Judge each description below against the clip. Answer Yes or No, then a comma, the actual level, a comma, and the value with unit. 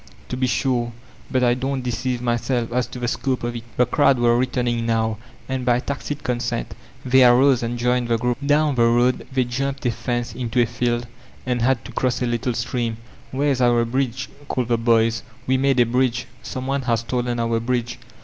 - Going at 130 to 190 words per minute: No, fast, 205 wpm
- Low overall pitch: Yes, low, 125 Hz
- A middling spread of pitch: No, narrow, 1.4 semitones